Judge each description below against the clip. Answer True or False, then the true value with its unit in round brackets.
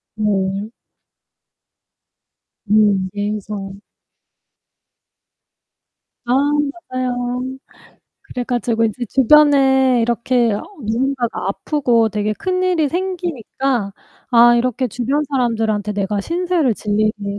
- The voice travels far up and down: False (4.0 semitones)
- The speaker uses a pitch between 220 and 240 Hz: True (235 Hz)